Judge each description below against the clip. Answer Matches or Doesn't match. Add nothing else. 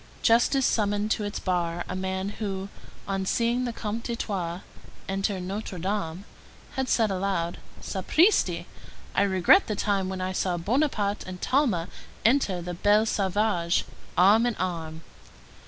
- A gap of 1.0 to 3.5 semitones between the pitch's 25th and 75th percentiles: Matches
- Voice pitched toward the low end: Doesn't match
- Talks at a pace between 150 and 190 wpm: Doesn't match